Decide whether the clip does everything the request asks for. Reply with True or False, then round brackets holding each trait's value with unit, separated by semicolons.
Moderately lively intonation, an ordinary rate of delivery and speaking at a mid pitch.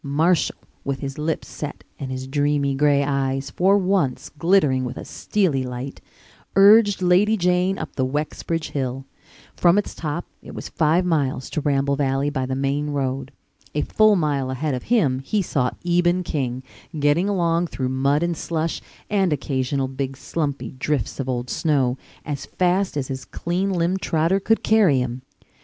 True (4.7 semitones; 170 wpm; 145 Hz)